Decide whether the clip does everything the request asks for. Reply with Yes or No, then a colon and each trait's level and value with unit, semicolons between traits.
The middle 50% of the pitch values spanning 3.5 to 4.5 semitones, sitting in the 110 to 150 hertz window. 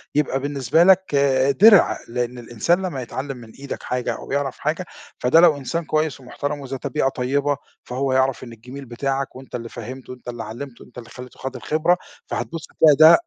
No: average, 3.1 semitones; low, 135 Hz